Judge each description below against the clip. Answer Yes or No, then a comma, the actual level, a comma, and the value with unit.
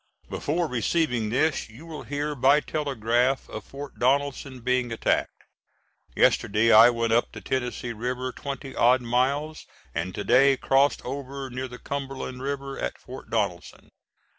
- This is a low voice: Yes, low, 130 Hz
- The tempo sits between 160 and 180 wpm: No, average, 145 wpm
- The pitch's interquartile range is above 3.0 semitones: No, average, 2.7 semitones